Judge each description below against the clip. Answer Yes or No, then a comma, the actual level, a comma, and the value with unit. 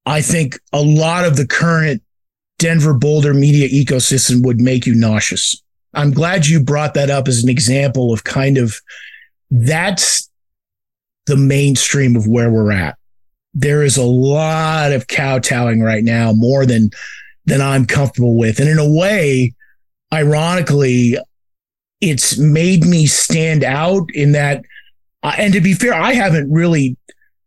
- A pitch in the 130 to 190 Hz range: Yes, medium, 140 Hz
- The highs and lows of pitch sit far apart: No, average, 4.2 semitones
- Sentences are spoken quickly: No, average, 145 wpm